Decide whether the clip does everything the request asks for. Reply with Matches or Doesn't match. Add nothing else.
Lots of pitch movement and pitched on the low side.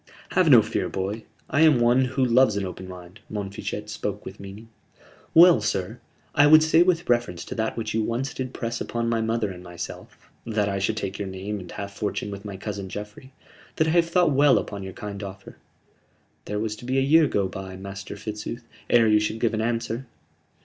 Doesn't match